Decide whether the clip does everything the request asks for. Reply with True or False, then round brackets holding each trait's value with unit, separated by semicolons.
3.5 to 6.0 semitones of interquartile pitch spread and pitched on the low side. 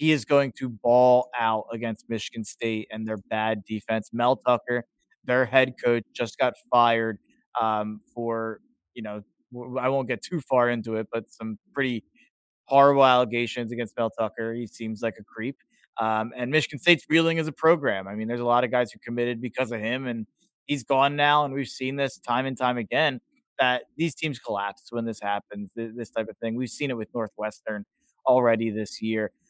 False (2.7 semitones; 120 Hz)